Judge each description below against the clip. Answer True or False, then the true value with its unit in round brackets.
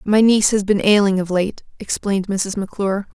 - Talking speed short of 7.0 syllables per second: True (5.9 syllables/s)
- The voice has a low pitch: False (200 Hz)